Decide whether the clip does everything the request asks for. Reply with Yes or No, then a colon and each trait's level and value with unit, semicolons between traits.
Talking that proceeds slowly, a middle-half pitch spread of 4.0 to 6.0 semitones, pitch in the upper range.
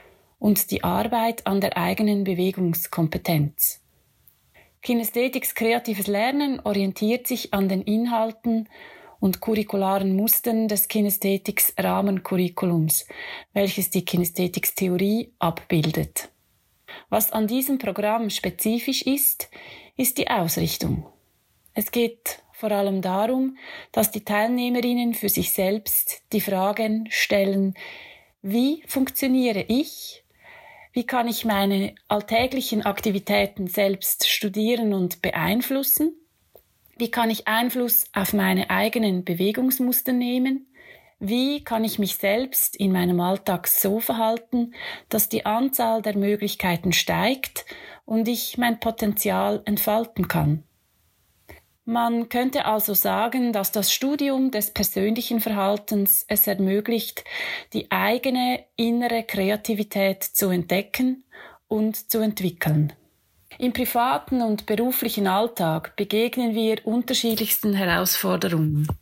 No: slow, 105 wpm; average, 3.4 semitones; high, 215 Hz